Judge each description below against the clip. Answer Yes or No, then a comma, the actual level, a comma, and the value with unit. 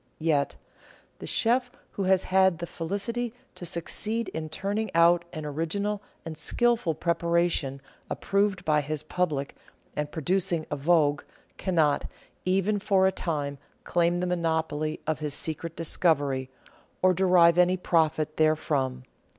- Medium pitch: Yes, medium, 170 Hz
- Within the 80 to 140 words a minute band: Yes, slow, 135 wpm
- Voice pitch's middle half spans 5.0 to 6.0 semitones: No, average, 3.5 semitones